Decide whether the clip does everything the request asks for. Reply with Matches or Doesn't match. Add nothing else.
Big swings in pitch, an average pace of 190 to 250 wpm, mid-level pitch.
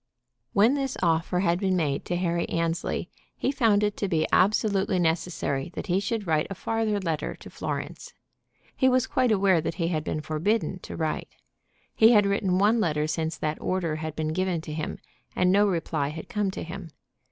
Doesn't match